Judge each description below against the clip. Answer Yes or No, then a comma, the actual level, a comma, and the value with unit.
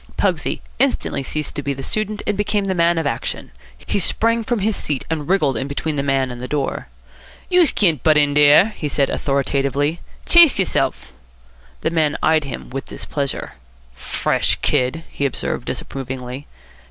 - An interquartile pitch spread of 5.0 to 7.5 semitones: Yes, wide, 5.5 semitones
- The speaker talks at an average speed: Yes, average, 170 wpm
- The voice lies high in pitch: No, medium, 150 Hz